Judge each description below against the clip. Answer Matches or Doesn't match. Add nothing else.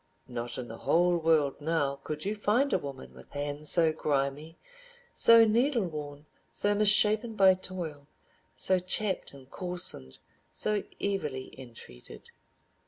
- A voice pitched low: Doesn't match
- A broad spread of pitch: Matches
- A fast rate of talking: Doesn't match